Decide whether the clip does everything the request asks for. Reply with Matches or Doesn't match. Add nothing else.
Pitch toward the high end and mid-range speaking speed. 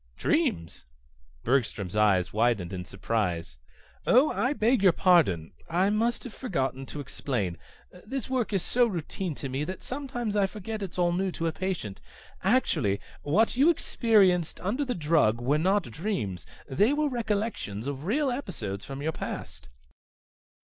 Doesn't match